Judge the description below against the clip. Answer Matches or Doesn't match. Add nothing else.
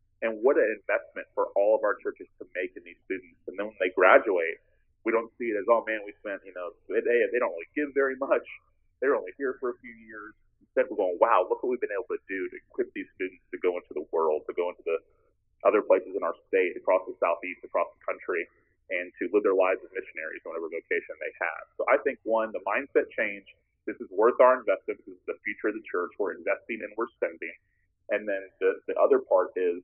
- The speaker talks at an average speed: Doesn't match